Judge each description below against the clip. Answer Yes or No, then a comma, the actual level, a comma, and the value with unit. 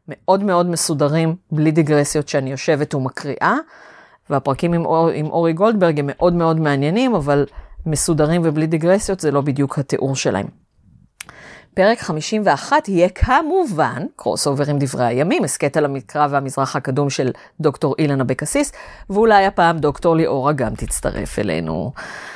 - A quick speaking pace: No, average, 140 wpm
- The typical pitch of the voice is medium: Yes, medium, 155 Hz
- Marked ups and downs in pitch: No, average, 3.5 semitones